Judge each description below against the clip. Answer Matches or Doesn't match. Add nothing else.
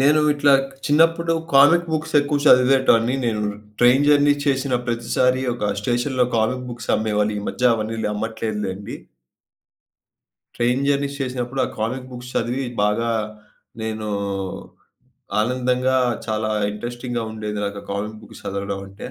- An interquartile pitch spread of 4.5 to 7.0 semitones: Doesn't match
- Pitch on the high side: Doesn't match